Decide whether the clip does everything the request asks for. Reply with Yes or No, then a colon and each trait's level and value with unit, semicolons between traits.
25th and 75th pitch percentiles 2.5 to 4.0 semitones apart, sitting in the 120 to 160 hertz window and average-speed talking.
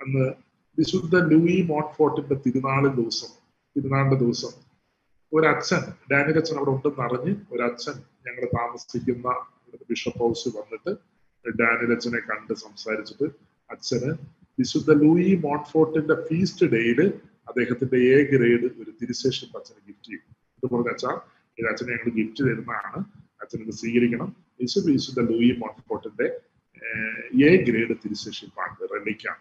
No: average, 4.8 semitones; low, 135 Hz; average, 110 wpm